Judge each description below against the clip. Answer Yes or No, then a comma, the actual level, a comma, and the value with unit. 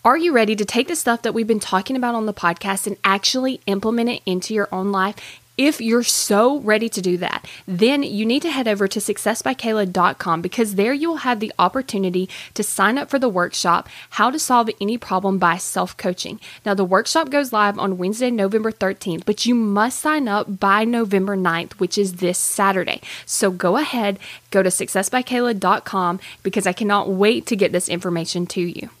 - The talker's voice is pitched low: No, high, 205 Hz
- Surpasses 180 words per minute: Yes, average, 200 wpm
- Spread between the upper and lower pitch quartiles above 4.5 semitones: No, average, 3.6 semitones